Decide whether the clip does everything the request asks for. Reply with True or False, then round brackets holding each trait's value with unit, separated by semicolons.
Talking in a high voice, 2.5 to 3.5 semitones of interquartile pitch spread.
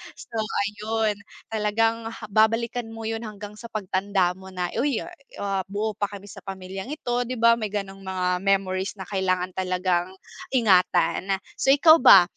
True (205 Hz; 2.9 semitones)